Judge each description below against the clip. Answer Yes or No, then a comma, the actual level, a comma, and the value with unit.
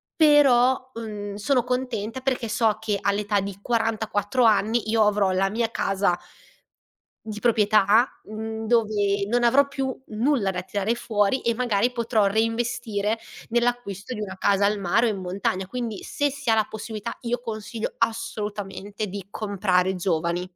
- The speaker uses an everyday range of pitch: Yes, average, 3.0 semitones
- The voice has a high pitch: Yes, high, 215 Hz